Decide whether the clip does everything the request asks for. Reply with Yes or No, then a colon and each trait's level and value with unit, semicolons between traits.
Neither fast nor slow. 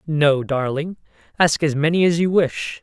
Yes: average, 170 wpm